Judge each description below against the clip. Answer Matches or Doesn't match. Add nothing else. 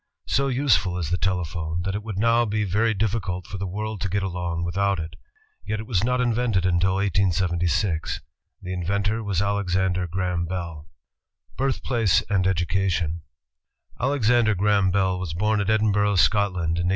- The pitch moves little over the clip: Doesn't match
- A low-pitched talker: Matches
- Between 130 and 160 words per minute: Doesn't match